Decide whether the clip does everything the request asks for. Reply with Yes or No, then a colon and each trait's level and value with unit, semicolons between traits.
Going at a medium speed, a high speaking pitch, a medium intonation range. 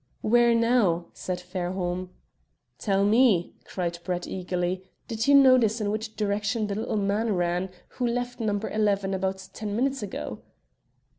Yes: average, 145 wpm; high, 205 Hz; average, 3.8 semitones